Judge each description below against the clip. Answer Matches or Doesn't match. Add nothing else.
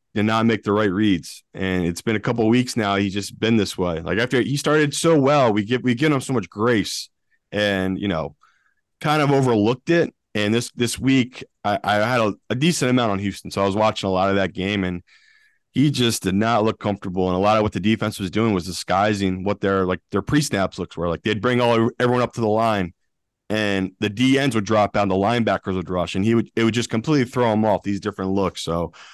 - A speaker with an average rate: Doesn't match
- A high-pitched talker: Doesn't match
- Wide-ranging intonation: Doesn't match